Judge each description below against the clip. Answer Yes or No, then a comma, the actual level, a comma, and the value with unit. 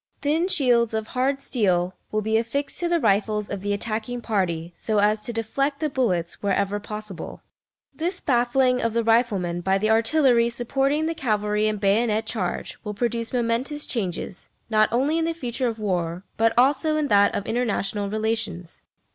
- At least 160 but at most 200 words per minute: Yes, average, 170 wpm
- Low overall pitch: No, high, 225 Hz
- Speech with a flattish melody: No, average, 3.8 semitones